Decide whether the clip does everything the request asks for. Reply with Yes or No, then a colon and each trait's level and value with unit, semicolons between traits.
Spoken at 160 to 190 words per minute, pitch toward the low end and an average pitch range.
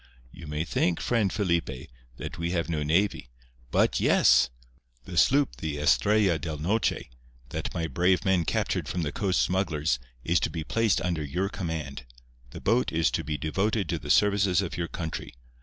Yes: average, 175 wpm; very low, 85 Hz; average, 4.3 semitones